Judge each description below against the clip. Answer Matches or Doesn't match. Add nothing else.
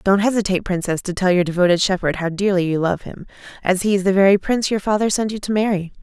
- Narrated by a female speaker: Matches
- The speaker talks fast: Matches